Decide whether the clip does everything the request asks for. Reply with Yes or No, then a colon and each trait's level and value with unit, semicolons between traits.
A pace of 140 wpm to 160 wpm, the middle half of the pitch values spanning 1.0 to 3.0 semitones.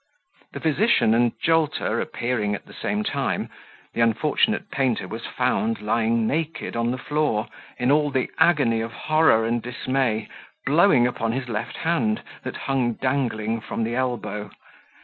No: average, 150 wpm; average, 4.6 semitones